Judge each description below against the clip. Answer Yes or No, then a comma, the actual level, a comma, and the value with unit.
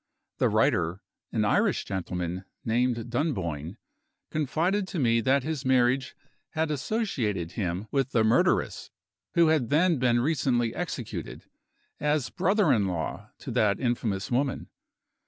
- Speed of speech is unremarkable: No, slow, 130 wpm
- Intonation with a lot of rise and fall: Yes, wide, 6.3 semitones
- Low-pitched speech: Yes, low, 125 Hz